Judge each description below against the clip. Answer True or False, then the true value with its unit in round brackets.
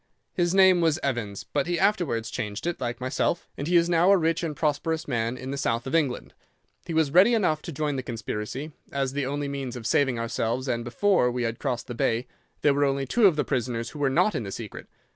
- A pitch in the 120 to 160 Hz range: True (140 Hz)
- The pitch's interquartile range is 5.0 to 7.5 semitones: True (5.4 semitones)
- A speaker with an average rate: False (240 wpm)